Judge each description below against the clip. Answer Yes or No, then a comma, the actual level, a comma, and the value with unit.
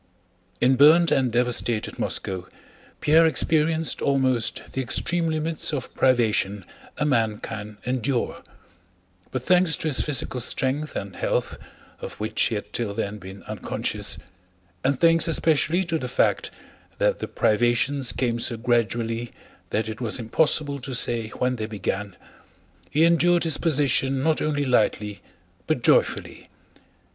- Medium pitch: No, low, 130 Hz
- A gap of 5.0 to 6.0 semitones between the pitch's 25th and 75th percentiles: Yes, average, 5.3 semitones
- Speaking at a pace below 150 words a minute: Yes, average, 140 wpm